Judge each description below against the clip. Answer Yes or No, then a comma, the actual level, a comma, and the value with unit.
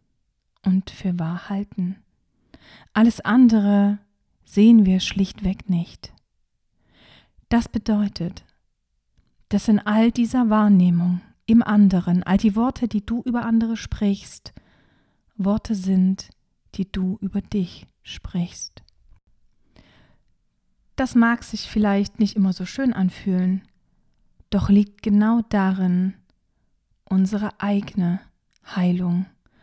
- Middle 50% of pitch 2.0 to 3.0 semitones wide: Yes, narrow, 2.6 semitones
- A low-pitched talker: No, high, 200 Hz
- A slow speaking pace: Yes, slow, 100 wpm